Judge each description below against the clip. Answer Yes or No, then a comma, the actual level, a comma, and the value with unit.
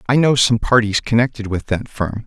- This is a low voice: Yes, low, 115 Hz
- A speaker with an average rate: No, fast, 210 wpm